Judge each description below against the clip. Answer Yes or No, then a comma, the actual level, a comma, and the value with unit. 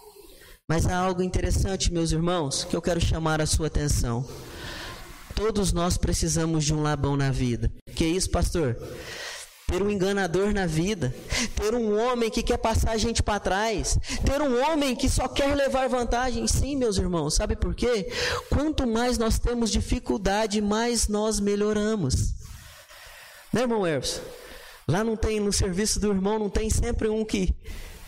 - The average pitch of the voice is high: Yes, high, 210 Hz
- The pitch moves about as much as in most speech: No, wide, 6.3 semitones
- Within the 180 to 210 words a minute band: No, average, 165 wpm